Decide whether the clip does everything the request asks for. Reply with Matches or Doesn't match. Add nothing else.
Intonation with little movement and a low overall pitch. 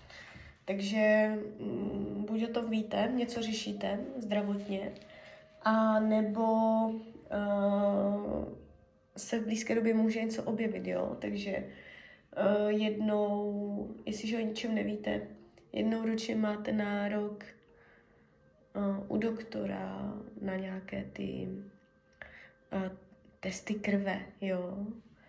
Doesn't match